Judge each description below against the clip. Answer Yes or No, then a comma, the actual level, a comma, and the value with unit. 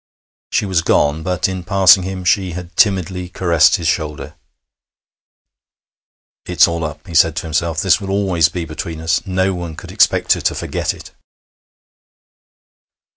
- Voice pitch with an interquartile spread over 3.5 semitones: No, narrow, 2.4 semitones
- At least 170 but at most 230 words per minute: No, average, 155 wpm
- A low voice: Yes, very low, 85 Hz